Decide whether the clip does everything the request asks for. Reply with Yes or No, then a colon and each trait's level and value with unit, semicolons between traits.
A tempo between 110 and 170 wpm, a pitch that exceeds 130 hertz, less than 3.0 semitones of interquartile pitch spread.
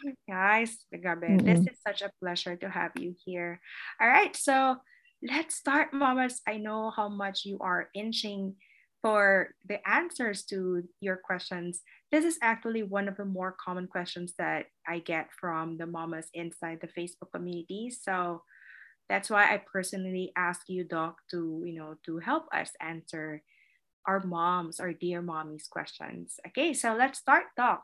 No: average, 160 wpm; medium, 185 Hz; average, 4.1 semitones